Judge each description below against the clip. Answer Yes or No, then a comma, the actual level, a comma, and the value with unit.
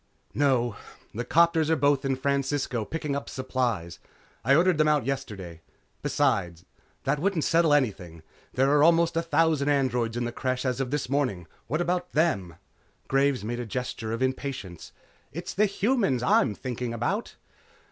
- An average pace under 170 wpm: Yes, average, 160 wpm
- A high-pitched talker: No, low, 135 Hz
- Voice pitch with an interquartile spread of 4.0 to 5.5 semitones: Yes, average, 4.5 semitones